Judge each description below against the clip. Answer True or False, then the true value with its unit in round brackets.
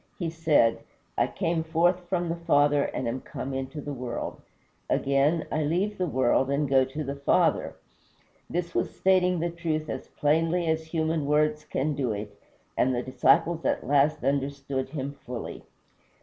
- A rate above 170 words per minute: False (165 wpm)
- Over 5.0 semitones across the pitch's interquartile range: False (3.4 semitones)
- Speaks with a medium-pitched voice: True (150 Hz)